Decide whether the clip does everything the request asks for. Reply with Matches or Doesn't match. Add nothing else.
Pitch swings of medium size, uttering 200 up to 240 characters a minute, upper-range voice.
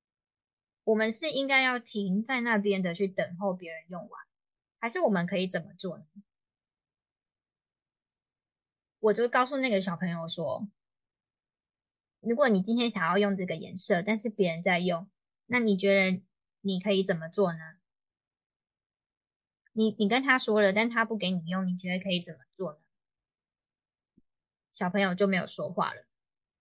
Matches